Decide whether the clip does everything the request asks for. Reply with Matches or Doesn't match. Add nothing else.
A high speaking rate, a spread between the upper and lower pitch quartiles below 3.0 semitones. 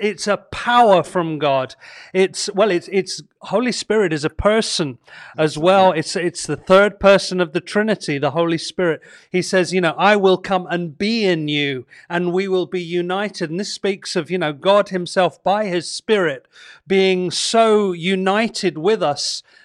Doesn't match